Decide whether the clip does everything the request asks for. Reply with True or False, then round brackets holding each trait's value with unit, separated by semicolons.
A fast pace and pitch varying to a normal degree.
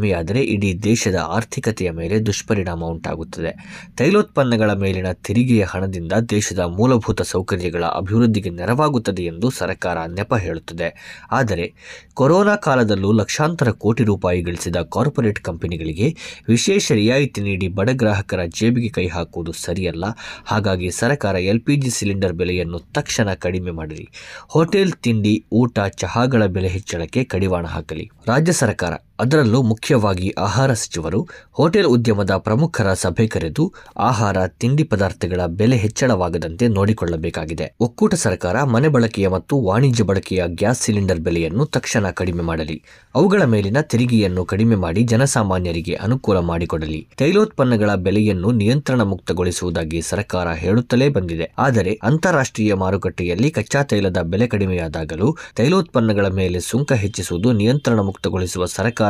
True (115 wpm; 4.8 semitones)